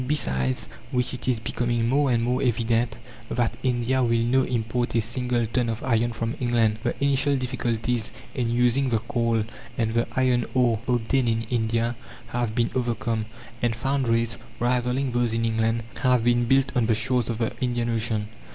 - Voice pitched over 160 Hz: No, low, 120 Hz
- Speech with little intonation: Yes, narrow, 1.6 semitones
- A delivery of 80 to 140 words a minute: No, average, 175 wpm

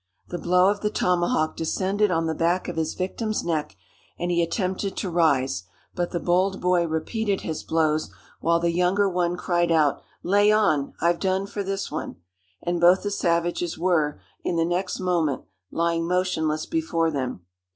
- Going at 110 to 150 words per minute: No, average, 170 wpm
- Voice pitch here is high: No, medium, 175 Hz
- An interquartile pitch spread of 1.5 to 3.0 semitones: Yes, narrow, 2.4 semitones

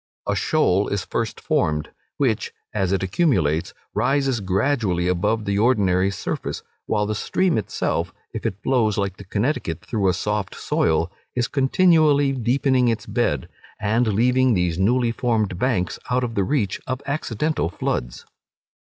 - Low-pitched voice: Yes, low, 110 Hz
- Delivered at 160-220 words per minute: No, average, 150 wpm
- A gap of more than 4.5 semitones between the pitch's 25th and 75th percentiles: Yes, average, 5.2 semitones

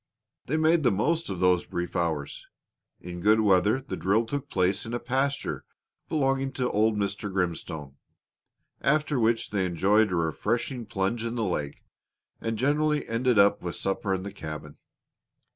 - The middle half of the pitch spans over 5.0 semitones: Yes, wide, 5.6 semitones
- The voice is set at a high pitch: No, low, 105 Hz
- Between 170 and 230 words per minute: No, average, 160 wpm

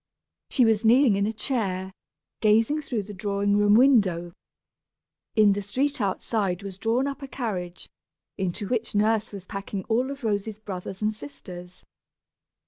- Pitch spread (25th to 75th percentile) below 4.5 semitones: Yes, average, 3.0 semitones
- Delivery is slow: No, average, 150 wpm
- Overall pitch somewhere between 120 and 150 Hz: No, high, 210 Hz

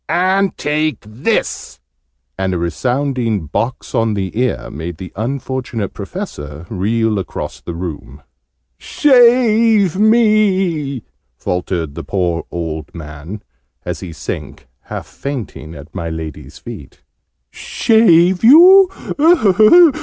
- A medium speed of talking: No, slow, 110 wpm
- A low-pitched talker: Yes, low, 115 Hz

